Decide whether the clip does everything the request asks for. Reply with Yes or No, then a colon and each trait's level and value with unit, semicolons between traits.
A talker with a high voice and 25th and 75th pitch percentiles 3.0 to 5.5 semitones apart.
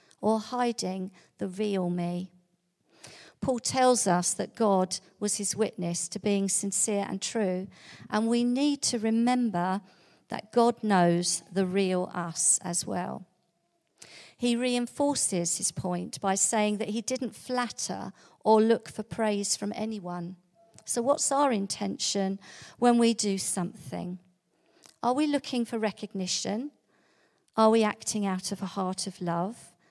Yes: high, 200 Hz; average, 4.0 semitones